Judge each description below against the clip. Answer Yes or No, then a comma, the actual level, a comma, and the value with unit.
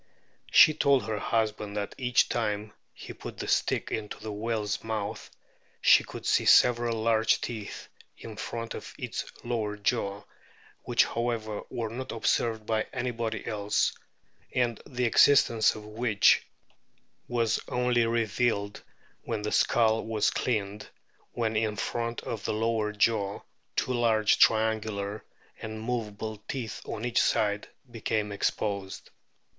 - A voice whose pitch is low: Yes, low, 110 Hz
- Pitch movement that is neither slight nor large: No, narrow, 1.8 semitones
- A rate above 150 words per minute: No, slow, 135 wpm